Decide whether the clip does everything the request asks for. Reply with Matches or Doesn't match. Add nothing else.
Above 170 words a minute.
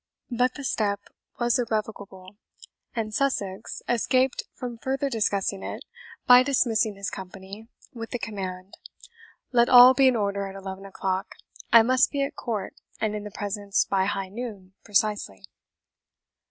Doesn't match